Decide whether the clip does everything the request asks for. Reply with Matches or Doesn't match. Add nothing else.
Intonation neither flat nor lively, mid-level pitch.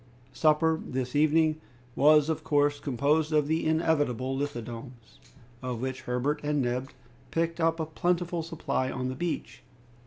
Matches